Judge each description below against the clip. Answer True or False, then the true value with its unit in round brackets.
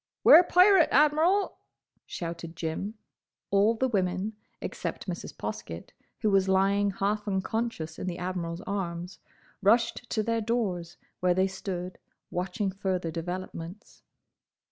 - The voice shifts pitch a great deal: False (3.8 semitones)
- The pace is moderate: False (120 wpm)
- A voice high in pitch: True (195 Hz)